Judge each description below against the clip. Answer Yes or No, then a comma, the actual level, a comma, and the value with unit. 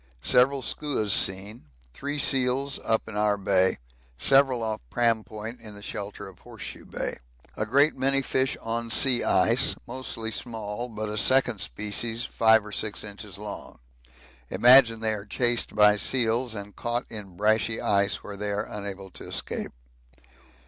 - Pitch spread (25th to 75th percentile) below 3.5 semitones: Yes, average, 3.1 semitones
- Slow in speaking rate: No, average, 160 wpm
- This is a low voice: Yes, low, 110 Hz